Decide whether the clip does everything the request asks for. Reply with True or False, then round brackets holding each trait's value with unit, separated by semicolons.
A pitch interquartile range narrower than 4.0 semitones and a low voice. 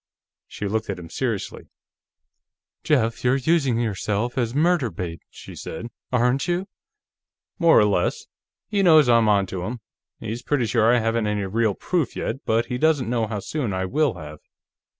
False (4.5 semitones; 115 Hz)